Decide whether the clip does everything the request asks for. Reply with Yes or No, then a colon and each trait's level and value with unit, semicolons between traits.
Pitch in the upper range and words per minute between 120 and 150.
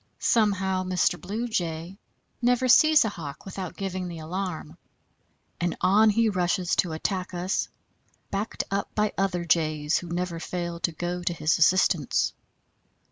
No: medium, 180 Hz; average, 145 wpm